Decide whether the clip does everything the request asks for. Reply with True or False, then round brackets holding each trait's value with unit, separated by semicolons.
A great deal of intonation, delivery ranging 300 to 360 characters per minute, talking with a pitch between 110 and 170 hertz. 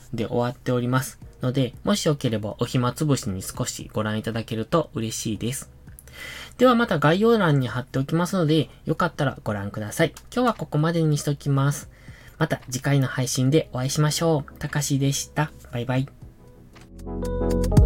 False (4.4 semitones; 355 characters per minute; 135 Hz)